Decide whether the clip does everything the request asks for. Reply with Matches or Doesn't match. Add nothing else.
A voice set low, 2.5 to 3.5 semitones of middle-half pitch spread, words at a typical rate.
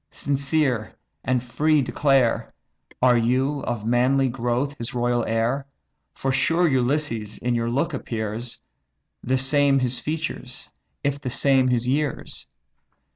Doesn't match